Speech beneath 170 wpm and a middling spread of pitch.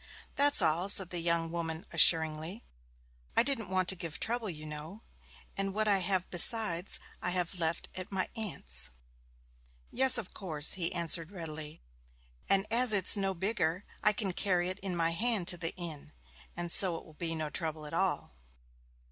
No: average, 175 wpm; average, 3.1 semitones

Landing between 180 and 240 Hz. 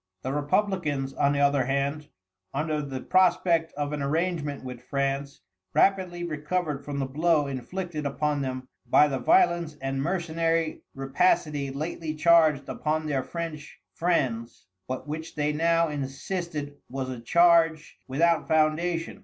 No: medium, 150 Hz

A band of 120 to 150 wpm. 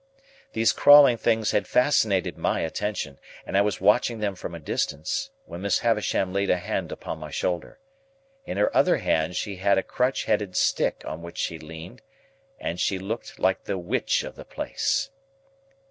No: average, 175 wpm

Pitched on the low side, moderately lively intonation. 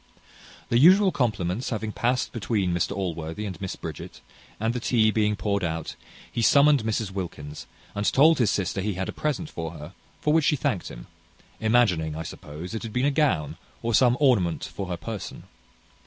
No: low, 105 Hz; wide, 5.8 semitones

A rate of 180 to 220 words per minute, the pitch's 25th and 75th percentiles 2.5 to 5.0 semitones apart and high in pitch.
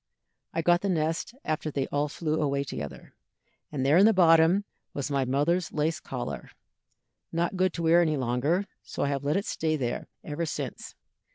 No: average, 185 wpm; average, 3.4 semitones; medium, 155 Hz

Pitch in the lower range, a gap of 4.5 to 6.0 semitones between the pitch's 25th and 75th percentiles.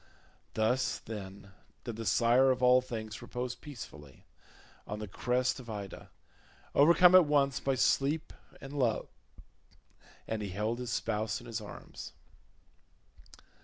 No: low, 120 Hz; average, 3.6 semitones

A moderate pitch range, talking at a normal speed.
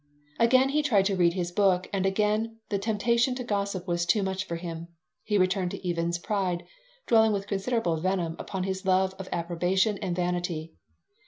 Yes: average, 3.0 semitones; average, 180 wpm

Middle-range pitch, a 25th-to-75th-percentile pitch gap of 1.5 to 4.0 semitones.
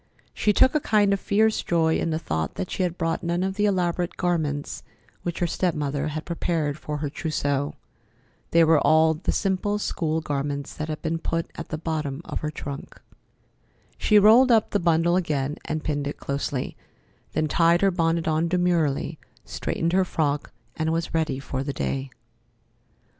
Yes: medium, 160 Hz; average, 3.1 semitones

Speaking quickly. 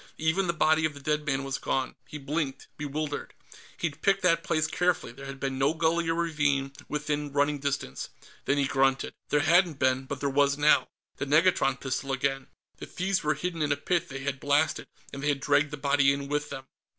Yes: fast, 210 wpm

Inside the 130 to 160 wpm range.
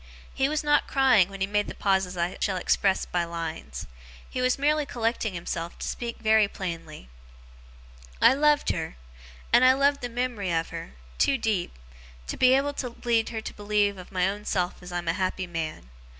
No: average, 195 wpm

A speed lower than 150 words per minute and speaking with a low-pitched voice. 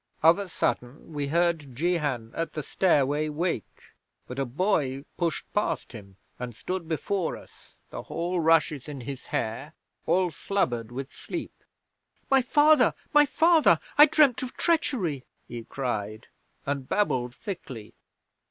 No: average, 140 wpm; medium, 155 Hz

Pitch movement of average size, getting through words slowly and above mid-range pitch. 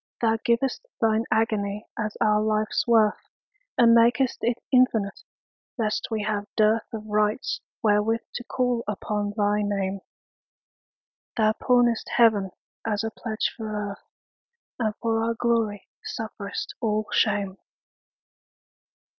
No: narrow, 1.9 semitones; slow, 110 wpm; high, 220 Hz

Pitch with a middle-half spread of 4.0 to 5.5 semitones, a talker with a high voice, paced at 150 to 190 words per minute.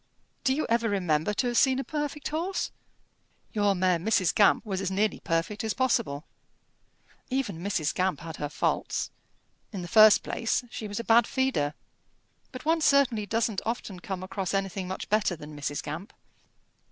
Yes: average, 5.0 semitones; high, 205 Hz; average, 170 wpm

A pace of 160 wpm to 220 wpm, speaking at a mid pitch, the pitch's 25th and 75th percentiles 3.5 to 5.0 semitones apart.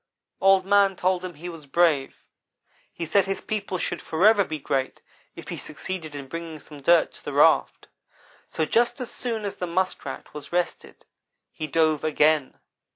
Yes: average, 170 wpm; medium, 170 Hz; average, 3.9 semitones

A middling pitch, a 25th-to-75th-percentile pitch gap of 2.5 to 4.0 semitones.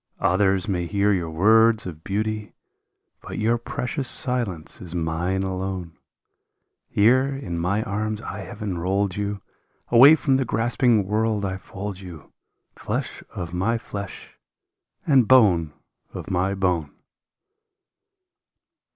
No: low, 100 Hz; average, 3.6 semitones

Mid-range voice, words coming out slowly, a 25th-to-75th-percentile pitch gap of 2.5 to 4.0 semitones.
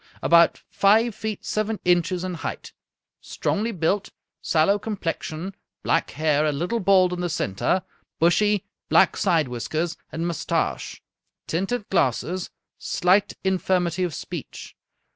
Yes: medium, 180 Hz; slow, 125 wpm; average, 3.3 semitones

